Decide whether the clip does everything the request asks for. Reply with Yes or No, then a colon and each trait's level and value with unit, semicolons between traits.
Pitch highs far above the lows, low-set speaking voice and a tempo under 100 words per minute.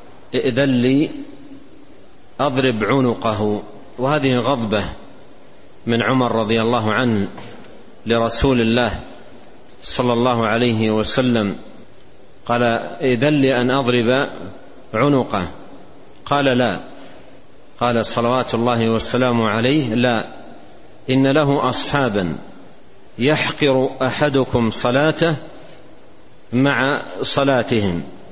No: average, 2.9 semitones; low, 125 Hz; average, 85 wpm